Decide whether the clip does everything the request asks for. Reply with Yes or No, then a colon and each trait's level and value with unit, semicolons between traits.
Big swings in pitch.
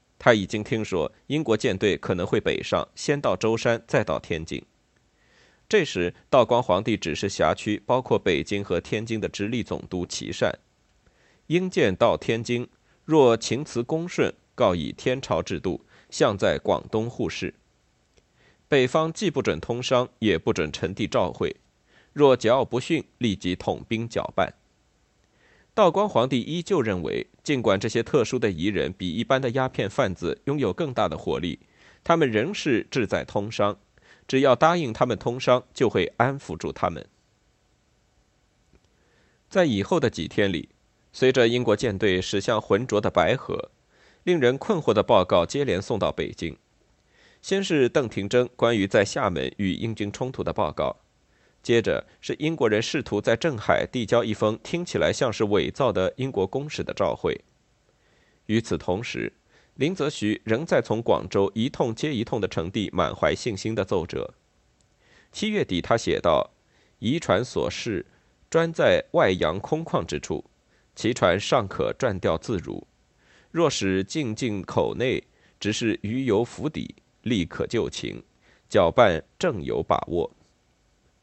No: average, 4.2 semitones